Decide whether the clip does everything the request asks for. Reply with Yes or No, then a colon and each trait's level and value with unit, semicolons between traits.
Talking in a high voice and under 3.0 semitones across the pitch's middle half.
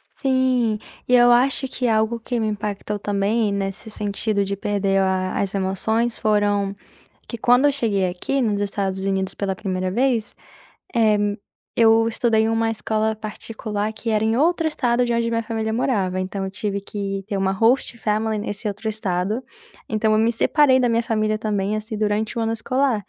Yes: high, 215 Hz; narrow, 2.5 semitones